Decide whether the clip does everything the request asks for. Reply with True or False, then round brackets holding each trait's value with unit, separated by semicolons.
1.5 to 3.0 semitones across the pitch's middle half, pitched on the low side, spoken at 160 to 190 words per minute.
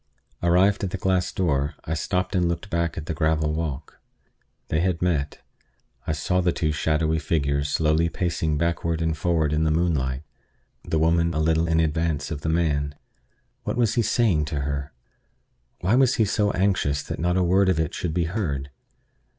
True (2.6 semitones; 80 Hz; 185 wpm)